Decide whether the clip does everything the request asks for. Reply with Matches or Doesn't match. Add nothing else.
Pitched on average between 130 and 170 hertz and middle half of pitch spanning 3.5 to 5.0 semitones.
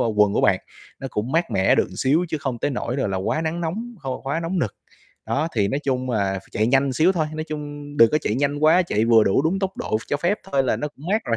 Doesn't match